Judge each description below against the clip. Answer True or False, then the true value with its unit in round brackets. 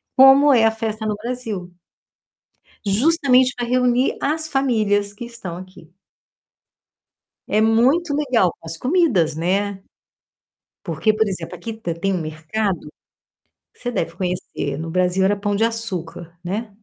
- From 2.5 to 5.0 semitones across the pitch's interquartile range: False (5.4 semitones)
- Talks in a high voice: True (215 Hz)